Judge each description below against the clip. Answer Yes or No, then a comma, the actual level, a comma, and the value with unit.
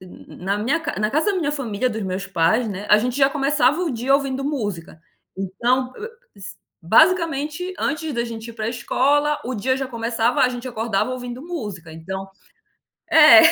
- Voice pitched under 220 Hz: No, high, 245 Hz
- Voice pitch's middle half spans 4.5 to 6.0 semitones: Yes, average, 5.2 semitones